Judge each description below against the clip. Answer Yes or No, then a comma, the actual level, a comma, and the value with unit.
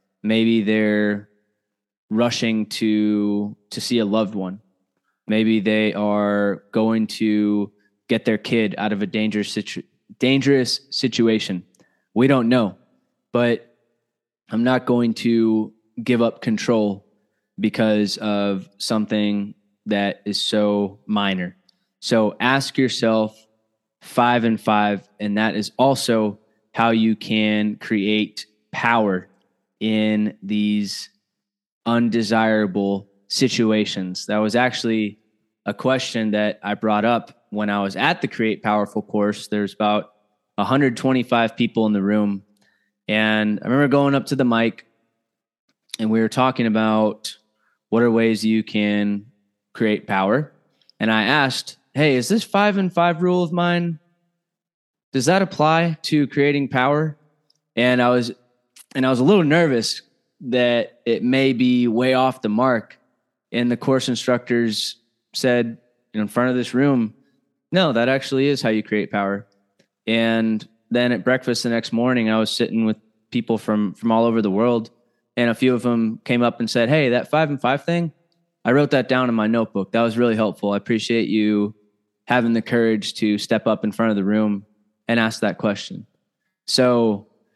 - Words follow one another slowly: No, average, 155 wpm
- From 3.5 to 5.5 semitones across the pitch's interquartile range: No, average, 2.8 semitones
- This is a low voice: Yes, low, 110 Hz